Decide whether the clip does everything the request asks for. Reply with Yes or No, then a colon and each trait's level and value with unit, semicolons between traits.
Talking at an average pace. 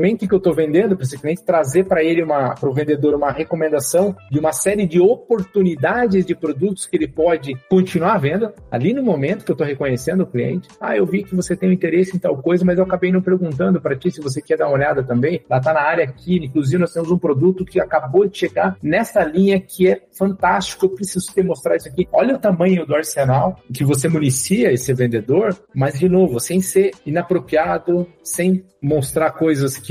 No: fast, 215 wpm